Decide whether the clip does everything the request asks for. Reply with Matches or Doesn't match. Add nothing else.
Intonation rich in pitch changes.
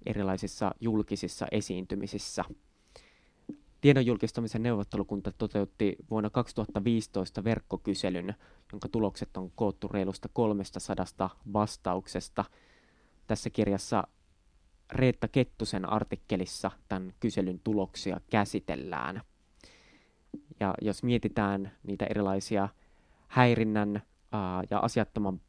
Doesn't match